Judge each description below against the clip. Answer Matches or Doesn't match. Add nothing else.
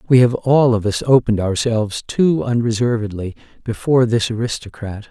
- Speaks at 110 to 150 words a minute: Matches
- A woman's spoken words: Doesn't match